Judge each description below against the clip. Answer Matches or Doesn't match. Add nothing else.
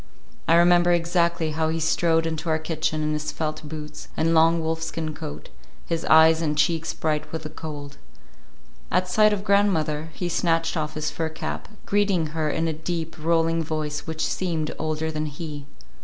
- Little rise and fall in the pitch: Matches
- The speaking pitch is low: Doesn't match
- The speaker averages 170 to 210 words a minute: Matches